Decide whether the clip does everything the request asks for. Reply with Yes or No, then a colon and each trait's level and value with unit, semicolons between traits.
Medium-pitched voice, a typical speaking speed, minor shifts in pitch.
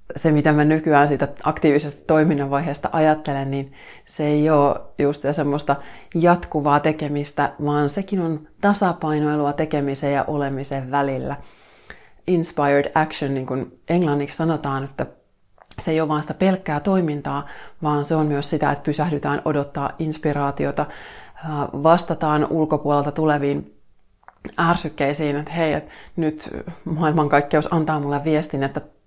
Yes: medium, 150 Hz; average, 125 wpm; narrow, 1.7 semitones